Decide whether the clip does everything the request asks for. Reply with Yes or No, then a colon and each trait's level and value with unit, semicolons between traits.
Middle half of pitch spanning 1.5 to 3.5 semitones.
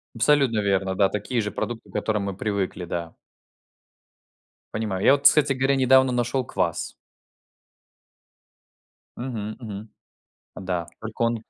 No: average, 4.5 semitones